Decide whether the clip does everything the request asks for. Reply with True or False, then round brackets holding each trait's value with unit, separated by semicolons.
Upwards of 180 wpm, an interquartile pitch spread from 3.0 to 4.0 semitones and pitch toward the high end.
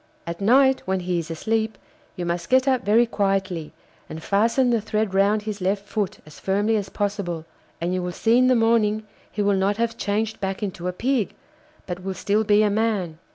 True (205 wpm; 3.3 semitones; 205 Hz)